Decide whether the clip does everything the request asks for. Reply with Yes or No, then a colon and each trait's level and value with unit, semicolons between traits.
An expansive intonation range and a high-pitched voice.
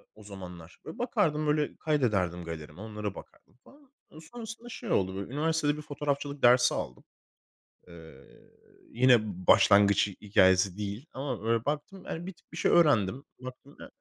No: wide, 7.5 semitones; low, 125 Hz